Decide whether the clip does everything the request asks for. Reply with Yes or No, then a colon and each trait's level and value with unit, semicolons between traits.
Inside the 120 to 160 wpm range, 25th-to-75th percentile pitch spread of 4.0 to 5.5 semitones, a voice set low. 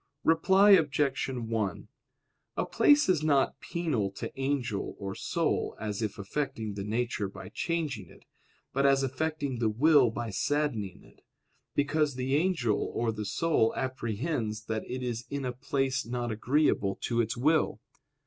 Yes: average, 150 wpm; average, 5.0 semitones; low, 130 Hz